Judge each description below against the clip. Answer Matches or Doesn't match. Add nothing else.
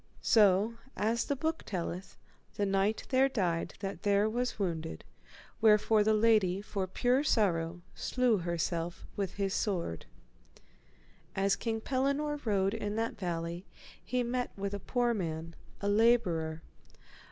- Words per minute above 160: Doesn't match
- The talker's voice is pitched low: Doesn't match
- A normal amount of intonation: Matches